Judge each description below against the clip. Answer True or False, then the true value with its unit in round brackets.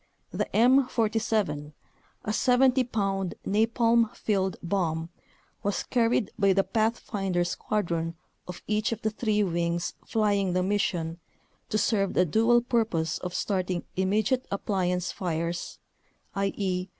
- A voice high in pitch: True (200 Hz)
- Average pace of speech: False (120 wpm)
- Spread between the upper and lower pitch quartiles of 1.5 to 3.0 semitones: False (3.7 semitones)